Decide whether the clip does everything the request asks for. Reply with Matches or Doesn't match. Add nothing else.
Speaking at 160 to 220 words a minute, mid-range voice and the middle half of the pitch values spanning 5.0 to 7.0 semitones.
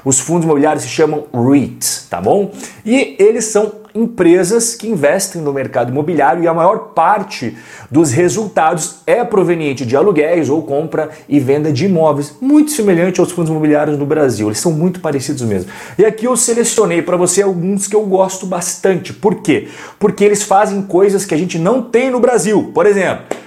Matches